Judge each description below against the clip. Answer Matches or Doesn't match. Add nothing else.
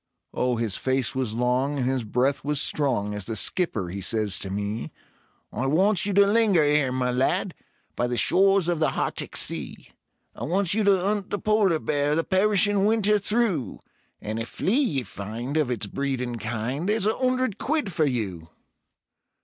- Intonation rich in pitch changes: Matches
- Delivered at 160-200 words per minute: Matches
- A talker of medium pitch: Matches